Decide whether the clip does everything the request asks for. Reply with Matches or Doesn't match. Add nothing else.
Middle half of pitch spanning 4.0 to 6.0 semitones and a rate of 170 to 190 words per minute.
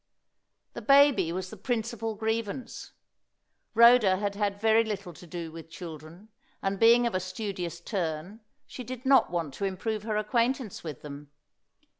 Doesn't match